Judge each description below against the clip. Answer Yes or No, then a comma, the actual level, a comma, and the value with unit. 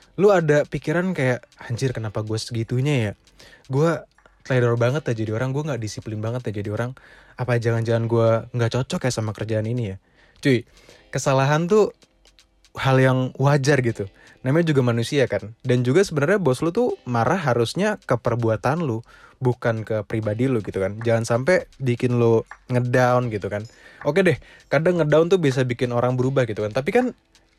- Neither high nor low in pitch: No, low, 125 Hz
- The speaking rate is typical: No, fast, 175 wpm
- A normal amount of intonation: Yes, average, 4.0 semitones